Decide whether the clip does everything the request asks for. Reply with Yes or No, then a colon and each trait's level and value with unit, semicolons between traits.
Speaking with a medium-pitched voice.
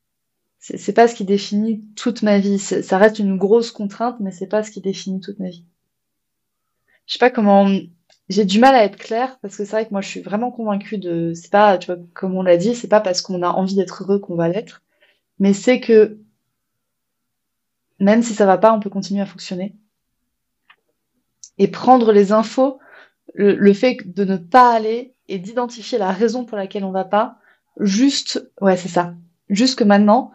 No: high, 205 Hz